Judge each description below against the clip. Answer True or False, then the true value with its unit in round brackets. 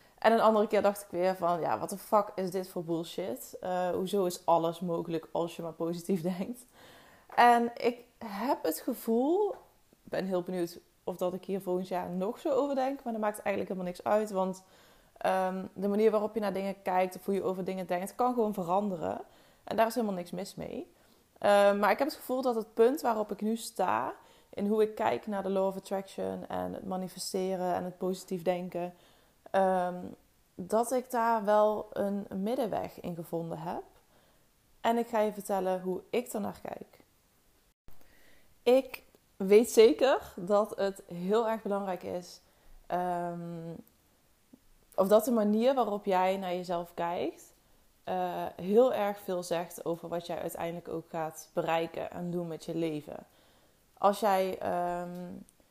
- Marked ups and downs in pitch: False (3.3 semitones)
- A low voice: False (190 Hz)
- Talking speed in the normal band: True (175 wpm)